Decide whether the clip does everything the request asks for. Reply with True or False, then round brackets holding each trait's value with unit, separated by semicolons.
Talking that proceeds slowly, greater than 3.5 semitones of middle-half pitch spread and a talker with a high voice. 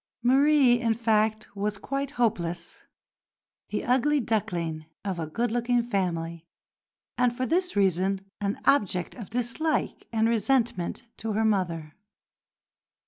True (125 wpm; 4.7 semitones; 220 Hz)